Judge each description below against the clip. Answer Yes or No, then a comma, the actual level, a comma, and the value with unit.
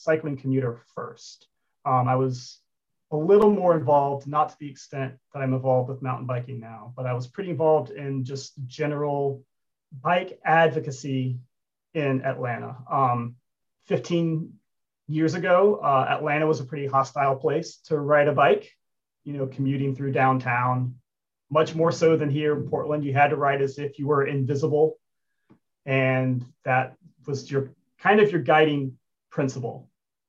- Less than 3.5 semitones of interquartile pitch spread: Yes, average, 2.9 semitones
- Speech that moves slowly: No, average, 155 wpm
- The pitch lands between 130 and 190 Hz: Yes, medium, 140 Hz